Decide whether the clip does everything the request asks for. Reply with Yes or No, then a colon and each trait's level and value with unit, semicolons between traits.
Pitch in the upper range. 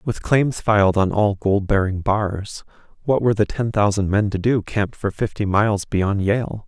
No: low, 105 Hz